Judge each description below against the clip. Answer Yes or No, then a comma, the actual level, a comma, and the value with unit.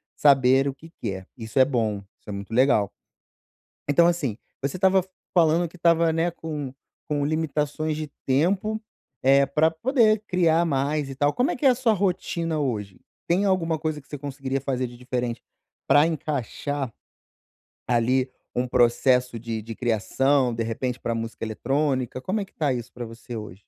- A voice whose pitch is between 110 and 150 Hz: Yes, medium, 140 Hz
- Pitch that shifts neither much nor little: Yes, average, 4.9 semitones